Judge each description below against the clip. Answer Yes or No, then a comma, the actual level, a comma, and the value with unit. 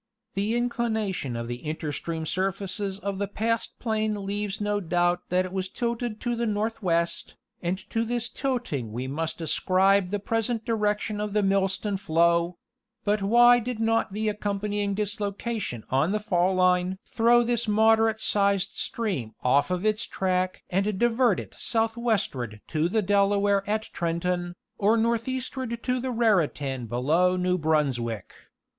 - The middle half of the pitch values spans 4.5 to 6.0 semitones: No, average, 4.0 semitones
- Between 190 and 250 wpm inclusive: No, average, 150 wpm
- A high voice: Yes, high, 200 Hz